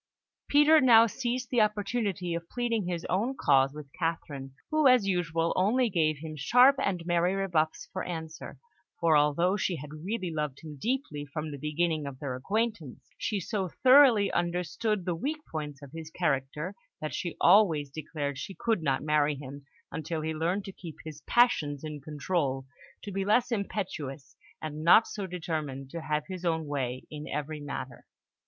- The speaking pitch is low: No, medium, 165 Hz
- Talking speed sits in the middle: Yes, average, 175 wpm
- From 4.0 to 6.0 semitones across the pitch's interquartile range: Yes, average, 5.1 semitones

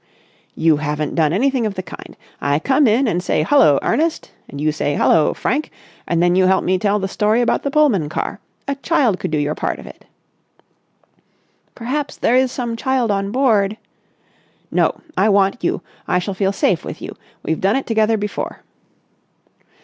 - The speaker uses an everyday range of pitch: No, wide, 6.3 semitones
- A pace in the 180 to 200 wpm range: Yes, average, 185 wpm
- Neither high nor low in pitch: No, high, 200 Hz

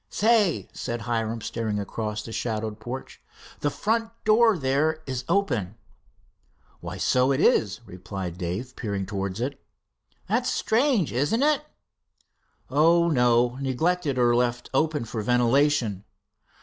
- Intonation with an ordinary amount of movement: No, wide, 6.3 semitones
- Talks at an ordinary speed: No, slow, 125 wpm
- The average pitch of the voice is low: Yes, low, 125 Hz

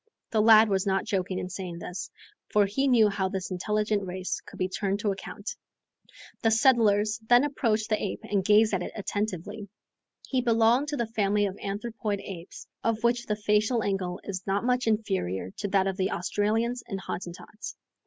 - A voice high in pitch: Yes, high, 210 Hz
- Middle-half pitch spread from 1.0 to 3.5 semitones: Yes, narrow, 2.6 semitones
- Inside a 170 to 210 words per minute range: Yes, average, 185 wpm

